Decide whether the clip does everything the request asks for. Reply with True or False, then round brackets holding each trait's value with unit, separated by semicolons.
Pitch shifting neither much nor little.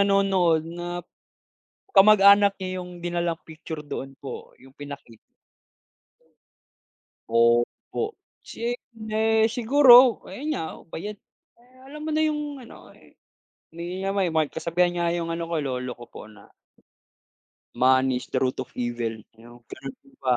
False (8.5 semitones)